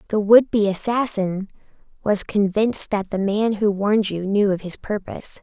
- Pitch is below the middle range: No, high, 205 Hz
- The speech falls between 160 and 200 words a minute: Yes, average, 175 wpm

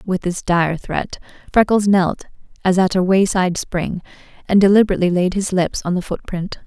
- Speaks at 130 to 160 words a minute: No, average, 170 wpm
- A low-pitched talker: No, medium, 185 Hz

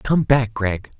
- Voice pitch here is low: Yes, low, 115 Hz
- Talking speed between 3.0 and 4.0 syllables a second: Yes, 3.3 syllables/s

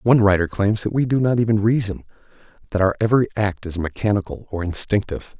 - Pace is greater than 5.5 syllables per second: Yes, 6.4 syllables/s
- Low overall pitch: Yes, low, 105 Hz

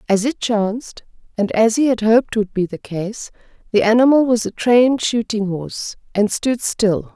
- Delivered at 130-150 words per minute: No, average, 185 wpm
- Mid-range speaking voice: No, high, 220 Hz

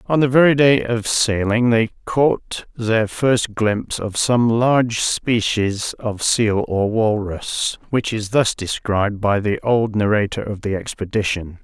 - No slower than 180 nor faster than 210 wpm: No, average, 155 wpm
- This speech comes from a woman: No, male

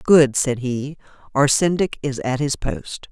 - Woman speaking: Yes, female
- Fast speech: No, average, 175 wpm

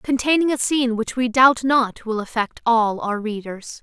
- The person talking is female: Yes, female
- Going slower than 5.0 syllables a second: Yes, 4.5 syllables/s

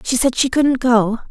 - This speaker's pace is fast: Yes, fast, 230 wpm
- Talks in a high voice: Yes, very high, 250 Hz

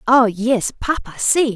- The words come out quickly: No, average, 155 wpm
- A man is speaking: No, female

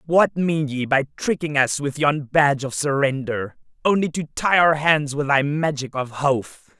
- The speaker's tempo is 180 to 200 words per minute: Yes, average, 185 wpm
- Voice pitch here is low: No, medium, 145 Hz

